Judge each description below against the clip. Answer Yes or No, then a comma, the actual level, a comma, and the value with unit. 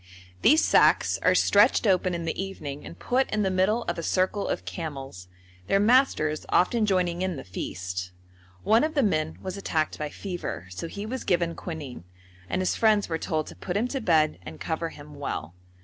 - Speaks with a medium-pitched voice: Yes, medium, 175 Hz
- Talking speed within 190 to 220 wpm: Yes, average, 195 wpm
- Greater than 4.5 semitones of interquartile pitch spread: Yes, average, 5.1 semitones